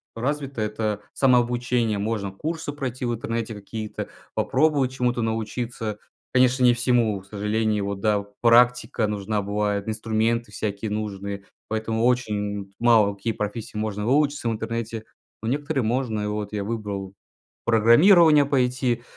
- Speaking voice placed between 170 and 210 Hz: No, low, 115 Hz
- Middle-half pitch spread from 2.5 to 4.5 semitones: Yes, average, 2.9 semitones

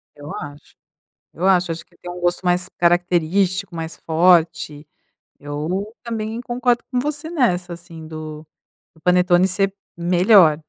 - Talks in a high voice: No, medium, 180 Hz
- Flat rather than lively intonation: No, average, 3.3 semitones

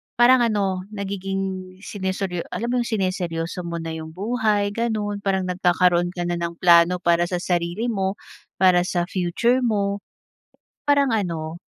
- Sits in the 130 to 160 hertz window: No, high, 190 Hz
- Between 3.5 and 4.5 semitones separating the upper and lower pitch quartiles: No, average, 2.9 semitones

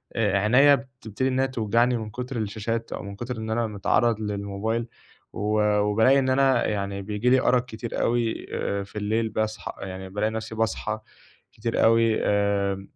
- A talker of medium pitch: No, low, 110 Hz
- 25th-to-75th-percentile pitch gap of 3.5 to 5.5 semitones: No, narrow, 2.5 semitones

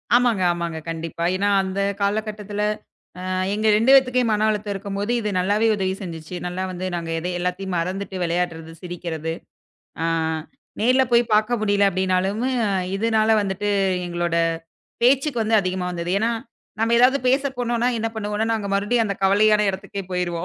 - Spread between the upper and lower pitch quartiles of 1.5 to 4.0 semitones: Yes, average, 3.4 semitones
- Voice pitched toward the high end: Yes, high, 200 Hz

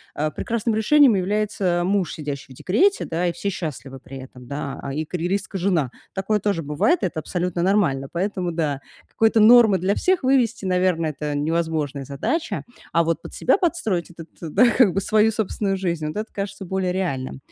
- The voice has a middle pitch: Yes, medium, 180 Hz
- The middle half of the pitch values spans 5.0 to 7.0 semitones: Yes, average, 5.3 semitones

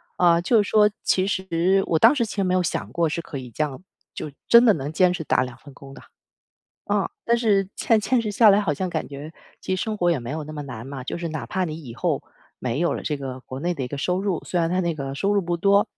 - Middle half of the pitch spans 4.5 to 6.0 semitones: Yes, wide, 5.5 semitones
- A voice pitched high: No, medium, 170 Hz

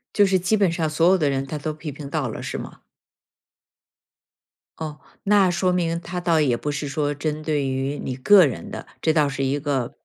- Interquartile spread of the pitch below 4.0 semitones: Yes, average, 3.6 semitones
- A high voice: No, medium, 155 Hz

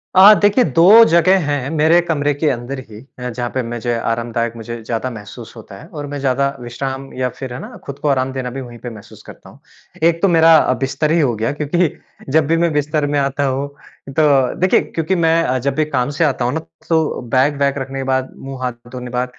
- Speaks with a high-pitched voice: No, low, 135 Hz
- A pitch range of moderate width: Yes, average, 3.8 semitones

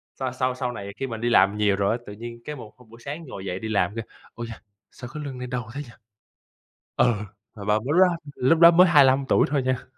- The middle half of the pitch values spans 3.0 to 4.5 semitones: Yes, average, 3.8 semitones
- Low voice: Yes, low, 125 Hz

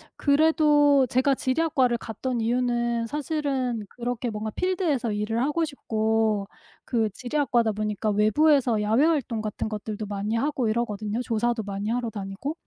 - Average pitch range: Yes, average, 4.4 semitones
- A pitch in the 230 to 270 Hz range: Yes, high, 235 Hz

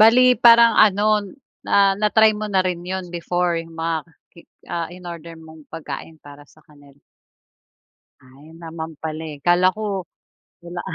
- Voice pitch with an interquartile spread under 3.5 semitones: Yes, average, 3.0 semitones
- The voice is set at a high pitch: No, medium, 170 Hz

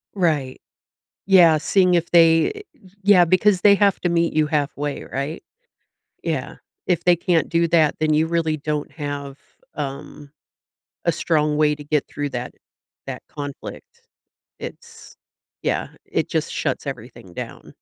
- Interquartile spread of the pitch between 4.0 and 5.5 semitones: No, average, 2.9 semitones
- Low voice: No, medium, 160 Hz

